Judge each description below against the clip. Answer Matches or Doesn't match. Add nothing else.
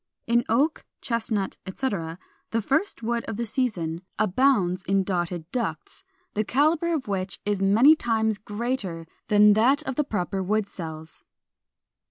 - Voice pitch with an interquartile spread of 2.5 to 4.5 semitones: Doesn't match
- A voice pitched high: Matches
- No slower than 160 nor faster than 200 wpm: Doesn't match